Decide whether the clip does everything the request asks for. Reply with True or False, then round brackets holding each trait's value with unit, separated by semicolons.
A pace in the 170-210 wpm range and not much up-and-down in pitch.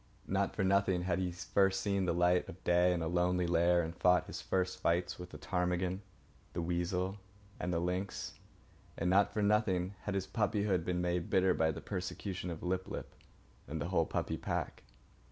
True (190 wpm; 1.4 semitones)